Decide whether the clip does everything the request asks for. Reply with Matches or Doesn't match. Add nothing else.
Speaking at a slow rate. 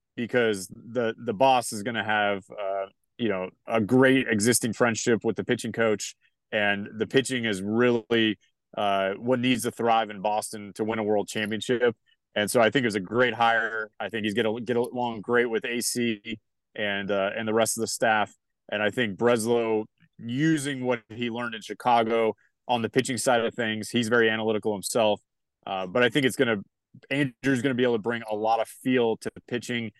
Doesn't match